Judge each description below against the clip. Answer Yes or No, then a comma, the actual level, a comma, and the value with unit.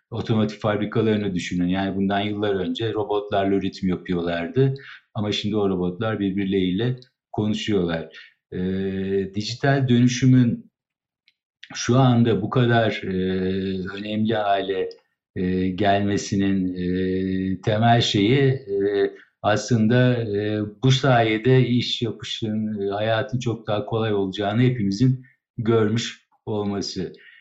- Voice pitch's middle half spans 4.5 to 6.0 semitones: No, average, 3.5 semitones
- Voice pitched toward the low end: Yes, low, 105 Hz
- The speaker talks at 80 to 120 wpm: Yes, average, 100 wpm